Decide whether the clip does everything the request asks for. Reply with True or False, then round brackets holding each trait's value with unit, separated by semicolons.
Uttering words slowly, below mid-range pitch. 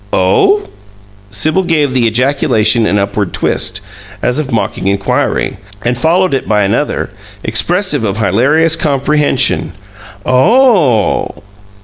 True (110 wpm; 130 Hz)